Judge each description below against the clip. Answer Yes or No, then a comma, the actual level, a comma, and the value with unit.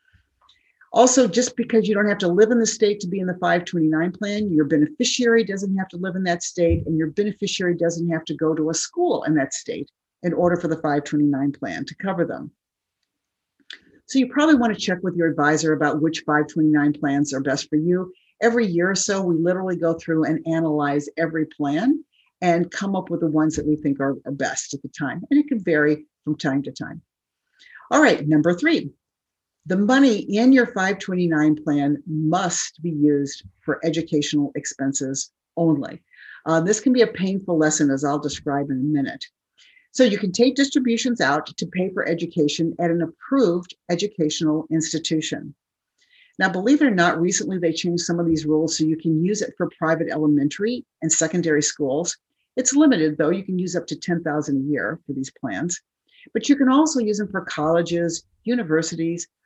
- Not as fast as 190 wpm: No, average, 195 wpm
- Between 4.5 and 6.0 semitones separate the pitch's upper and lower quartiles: Yes, average, 5.0 semitones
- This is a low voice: No, medium, 170 Hz